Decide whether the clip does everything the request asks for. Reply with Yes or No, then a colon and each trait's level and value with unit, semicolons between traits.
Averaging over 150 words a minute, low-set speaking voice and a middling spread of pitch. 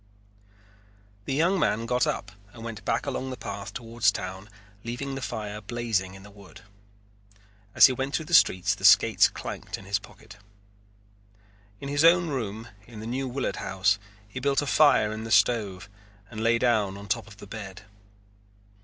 Yes: average, 180 wpm; low, 115 Hz; average, 4.2 semitones